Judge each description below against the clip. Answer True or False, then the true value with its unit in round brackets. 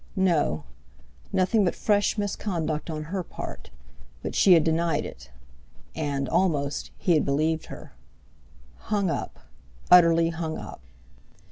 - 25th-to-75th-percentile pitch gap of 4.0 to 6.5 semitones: False (3.4 semitones)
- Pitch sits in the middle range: True (165 Hz)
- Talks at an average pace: False (110 wpm)